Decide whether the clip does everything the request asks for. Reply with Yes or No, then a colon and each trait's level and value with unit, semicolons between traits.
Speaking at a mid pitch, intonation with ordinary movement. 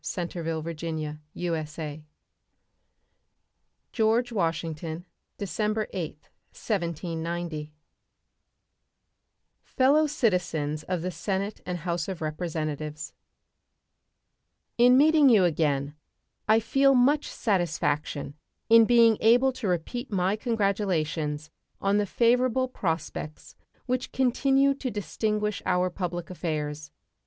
No: medium, 180 Hz; wide, 6.3 semitones